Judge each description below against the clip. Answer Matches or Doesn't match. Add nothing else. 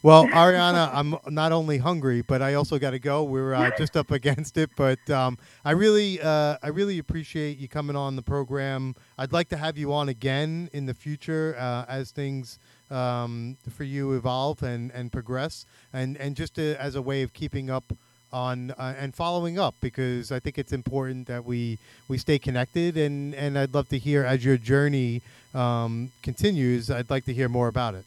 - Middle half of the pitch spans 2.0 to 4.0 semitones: Matches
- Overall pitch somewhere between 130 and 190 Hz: Matches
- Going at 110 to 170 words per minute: Doesn't match